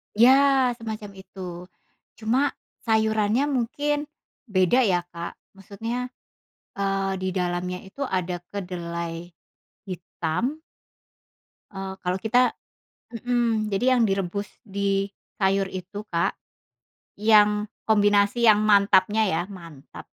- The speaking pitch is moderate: No, high, 200 Hz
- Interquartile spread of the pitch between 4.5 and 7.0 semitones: No, average, 2.8 semitones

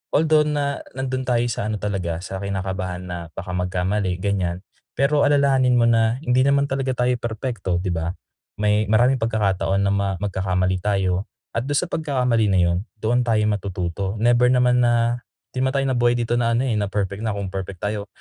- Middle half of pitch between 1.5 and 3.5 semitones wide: No, average, 4.5 semitones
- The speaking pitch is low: Yes, low, 105 Hz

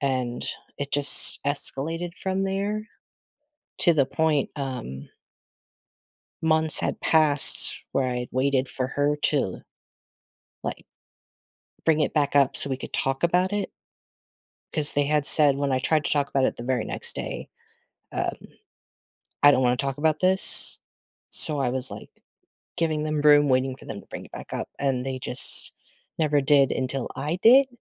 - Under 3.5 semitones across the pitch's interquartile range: Yes, average, 3.1 semitones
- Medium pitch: Yes, medium, 145 Hz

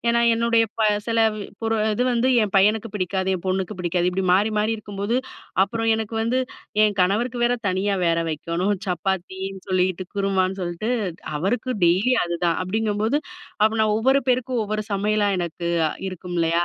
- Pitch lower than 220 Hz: Yes, high, 200 Hz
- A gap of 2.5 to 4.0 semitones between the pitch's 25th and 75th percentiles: Yes, average, 3.4 semitones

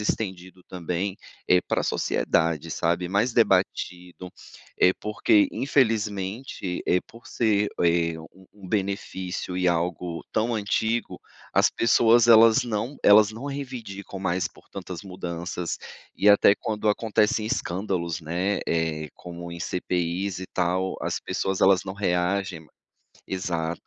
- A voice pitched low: Yes, very low, 95 Hz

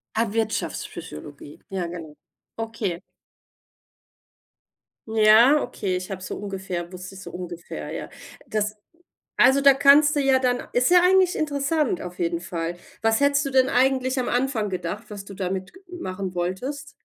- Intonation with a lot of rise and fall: Yes, wide, 6.7 semitones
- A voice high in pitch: Yes, high, 215 Hz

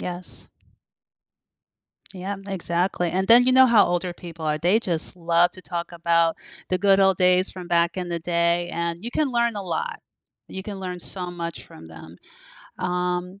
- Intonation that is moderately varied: No, narrow, 2.2 semitones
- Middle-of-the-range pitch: Yes, medium, 180 Hz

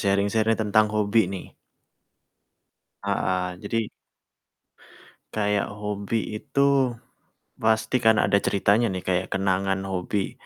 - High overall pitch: No, low, 105 Hz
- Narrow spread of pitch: Yes, narrow, 2.3 semitones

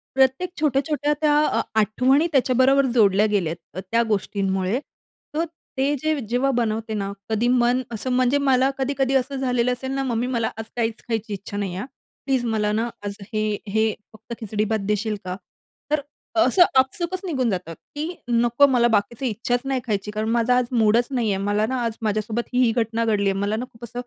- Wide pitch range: No, average, 3.6 semitones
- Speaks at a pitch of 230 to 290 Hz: Yes, high, 235 Hz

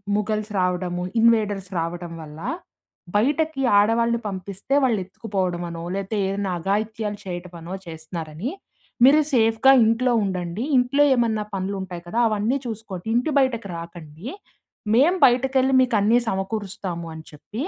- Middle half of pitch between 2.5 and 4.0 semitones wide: No, average, 4.7 semitones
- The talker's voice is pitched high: Yes, high, 205 Hz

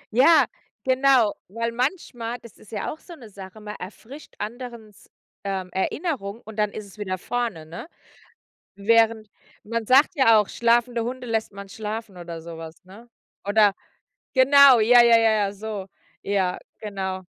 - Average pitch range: Yes, average, 3.4 semitones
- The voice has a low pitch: No, high, 220 Hz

